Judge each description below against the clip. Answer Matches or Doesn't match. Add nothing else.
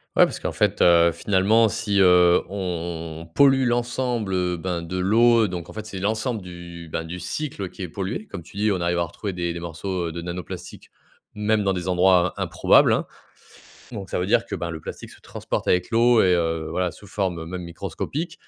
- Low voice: Matches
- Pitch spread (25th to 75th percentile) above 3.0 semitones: Matches